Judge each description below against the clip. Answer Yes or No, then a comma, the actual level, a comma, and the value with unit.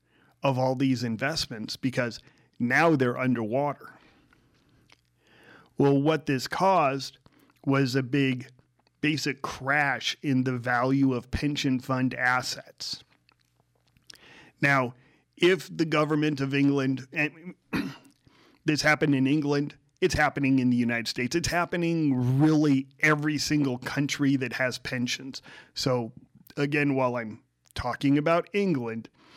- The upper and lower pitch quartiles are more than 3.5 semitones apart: No, average, 3.1 semitones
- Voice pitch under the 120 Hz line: No, low, 135 Hz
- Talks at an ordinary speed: No, slow, 115 wpm